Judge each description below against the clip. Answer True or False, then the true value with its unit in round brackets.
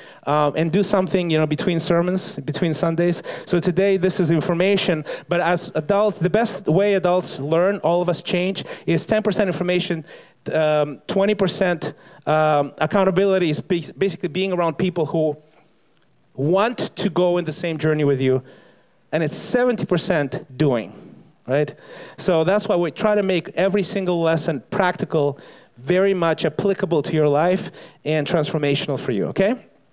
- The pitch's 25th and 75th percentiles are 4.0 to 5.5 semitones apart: False (3.6 semitones)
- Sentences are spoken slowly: False (155 wpm)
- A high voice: False (175 Hz)